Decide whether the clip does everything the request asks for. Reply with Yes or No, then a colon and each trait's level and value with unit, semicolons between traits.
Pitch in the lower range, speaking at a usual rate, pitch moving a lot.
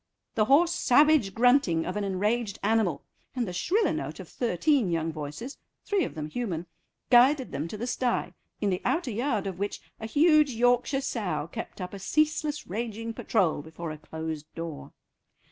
No: high, 220 Hz; average, 175 wpm; wide, 7.0 semitones